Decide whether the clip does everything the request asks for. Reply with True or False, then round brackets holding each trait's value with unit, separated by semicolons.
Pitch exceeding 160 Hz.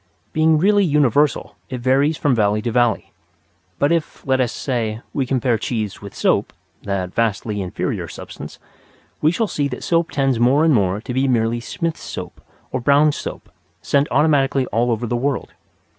False (130 Hz)